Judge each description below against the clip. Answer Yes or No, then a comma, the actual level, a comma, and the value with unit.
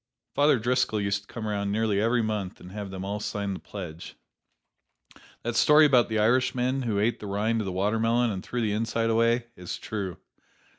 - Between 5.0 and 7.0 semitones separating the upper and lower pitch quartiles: No, average, 2.7 semitones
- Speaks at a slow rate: No, average, 195 wpm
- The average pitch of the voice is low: Yes, low, 110 Hz